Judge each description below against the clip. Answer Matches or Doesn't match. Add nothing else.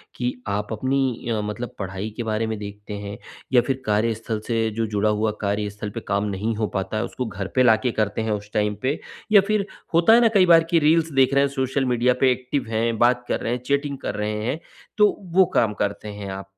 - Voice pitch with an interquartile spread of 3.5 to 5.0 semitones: Matches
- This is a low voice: Matches